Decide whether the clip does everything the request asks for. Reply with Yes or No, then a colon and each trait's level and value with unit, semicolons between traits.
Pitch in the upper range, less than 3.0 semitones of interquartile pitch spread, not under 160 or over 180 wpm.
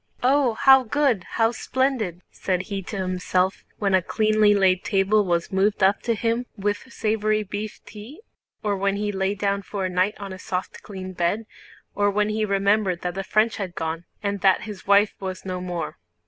No: high, 200 Hz; narrow, 2.4 semitones; average, 190 wpm